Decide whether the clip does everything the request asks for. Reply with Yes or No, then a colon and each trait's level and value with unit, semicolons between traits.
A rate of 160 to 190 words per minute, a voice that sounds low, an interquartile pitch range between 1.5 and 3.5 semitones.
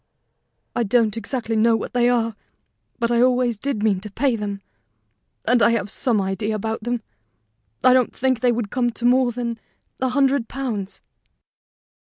No: average, 170 wpm; high, 235 Hz; narrow, 2.5 semitones